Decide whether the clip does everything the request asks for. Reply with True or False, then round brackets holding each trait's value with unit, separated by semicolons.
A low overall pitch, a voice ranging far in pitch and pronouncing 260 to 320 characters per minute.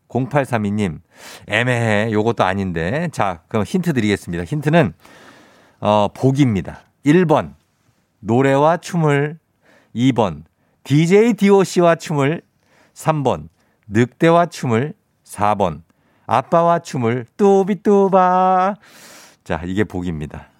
False (125 Hz; 8.4 semitones; 195 characters per minute)